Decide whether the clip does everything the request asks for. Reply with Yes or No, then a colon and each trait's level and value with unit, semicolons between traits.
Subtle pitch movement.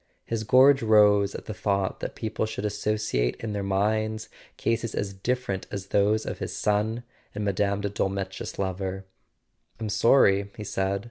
Yes: narrow, 1.9 semitones